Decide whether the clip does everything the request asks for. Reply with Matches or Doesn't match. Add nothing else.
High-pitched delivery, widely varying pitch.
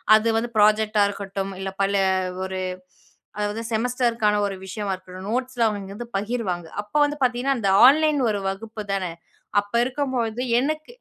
Doesn't match